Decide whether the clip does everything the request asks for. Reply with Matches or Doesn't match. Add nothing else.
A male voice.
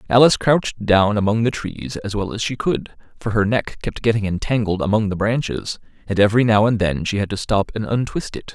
Matches